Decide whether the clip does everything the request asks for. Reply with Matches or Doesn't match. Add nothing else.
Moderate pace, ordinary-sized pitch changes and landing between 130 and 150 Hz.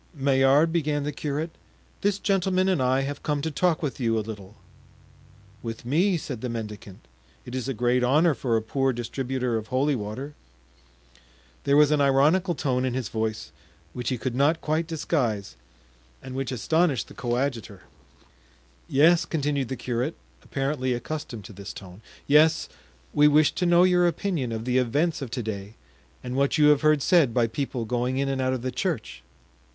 Matches